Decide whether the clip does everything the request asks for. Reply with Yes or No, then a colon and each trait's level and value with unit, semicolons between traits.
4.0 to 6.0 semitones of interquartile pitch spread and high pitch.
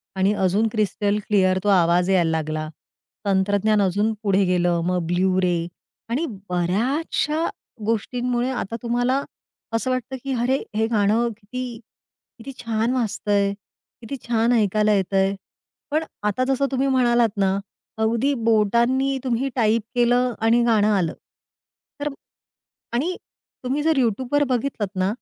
Yes: average, 4.3 semitones; high, 225 Hz